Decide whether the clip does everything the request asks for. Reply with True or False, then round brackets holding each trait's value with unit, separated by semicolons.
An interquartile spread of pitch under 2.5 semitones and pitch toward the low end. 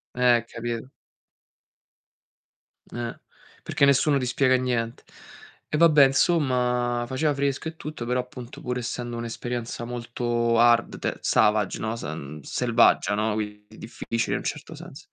True (1.8 semitones; 120 Hz)